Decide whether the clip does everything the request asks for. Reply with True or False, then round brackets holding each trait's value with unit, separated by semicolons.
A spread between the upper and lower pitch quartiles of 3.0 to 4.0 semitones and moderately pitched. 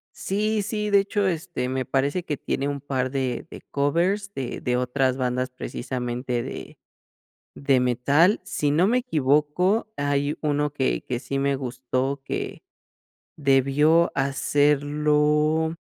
True (3.6 semitones; 145 Hz)